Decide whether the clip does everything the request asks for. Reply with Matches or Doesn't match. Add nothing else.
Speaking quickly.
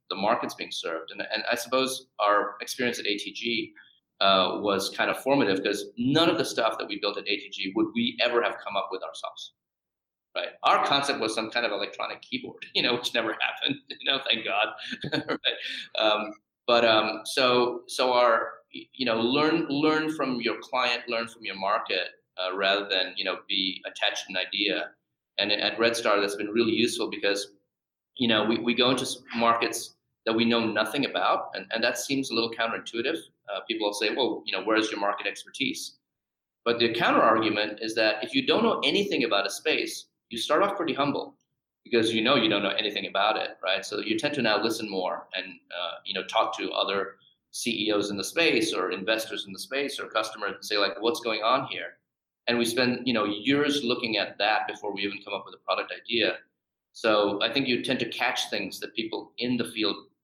Matches